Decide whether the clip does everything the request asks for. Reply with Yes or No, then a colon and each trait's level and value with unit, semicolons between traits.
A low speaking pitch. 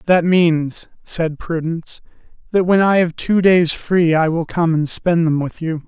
No: medium, 170 Hz